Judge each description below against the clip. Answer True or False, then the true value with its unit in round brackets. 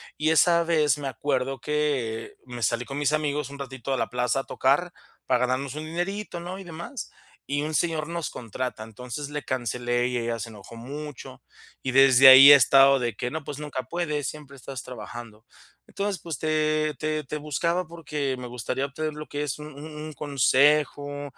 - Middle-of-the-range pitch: True (145 Hz)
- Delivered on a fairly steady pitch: False (3.2 semitones)